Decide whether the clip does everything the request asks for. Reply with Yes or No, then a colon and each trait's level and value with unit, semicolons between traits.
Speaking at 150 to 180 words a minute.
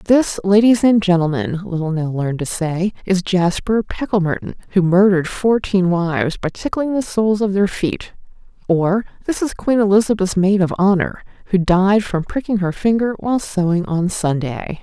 Yes: average, 165 wpm